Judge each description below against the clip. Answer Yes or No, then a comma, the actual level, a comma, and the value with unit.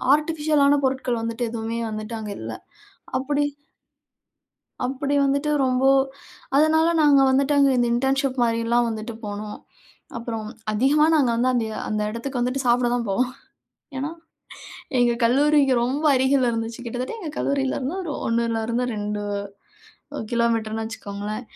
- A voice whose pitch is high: Yes, very high, 250 Hz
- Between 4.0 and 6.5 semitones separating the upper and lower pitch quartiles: No, average, 3.4 semitones